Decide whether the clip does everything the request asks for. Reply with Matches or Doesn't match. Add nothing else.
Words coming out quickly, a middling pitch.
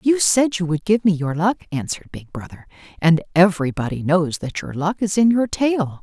Matches